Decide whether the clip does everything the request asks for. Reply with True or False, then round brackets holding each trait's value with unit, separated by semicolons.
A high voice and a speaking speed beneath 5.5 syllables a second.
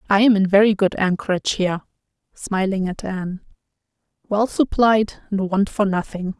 True (195 Hz; 5.0 syllables/s)